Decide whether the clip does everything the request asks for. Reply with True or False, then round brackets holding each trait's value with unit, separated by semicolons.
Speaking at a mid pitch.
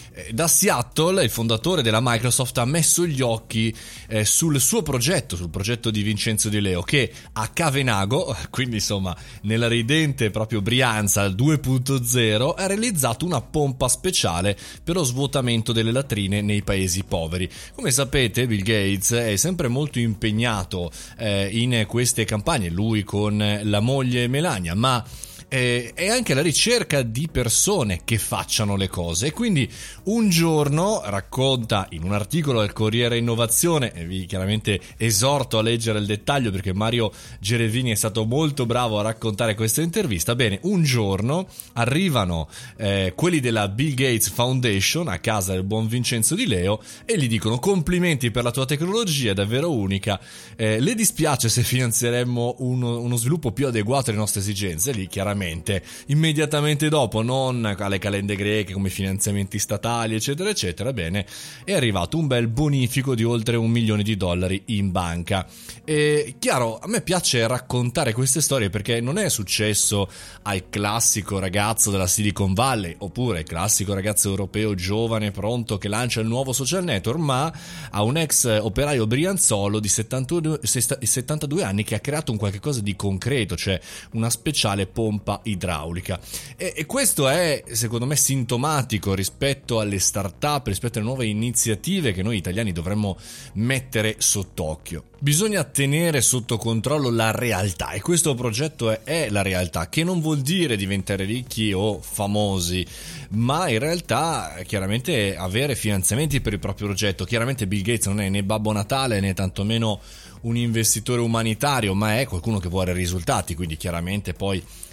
False (115 Hz)